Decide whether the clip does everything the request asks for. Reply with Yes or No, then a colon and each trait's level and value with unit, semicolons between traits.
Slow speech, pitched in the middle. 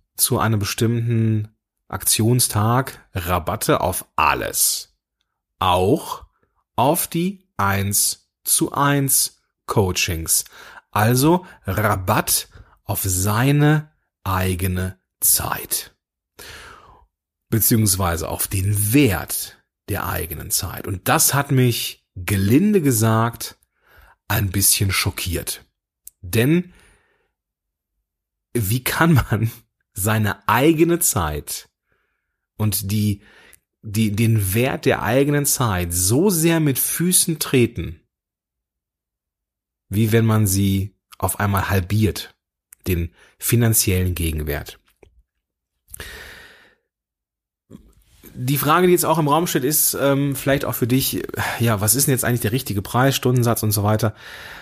No: slow, 100 wpm; low, 110 Hz